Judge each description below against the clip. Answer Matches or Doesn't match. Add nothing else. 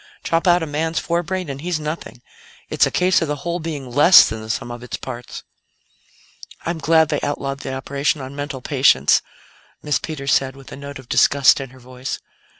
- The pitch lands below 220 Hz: Matches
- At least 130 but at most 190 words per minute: Doesn't match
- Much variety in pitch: Doesn't match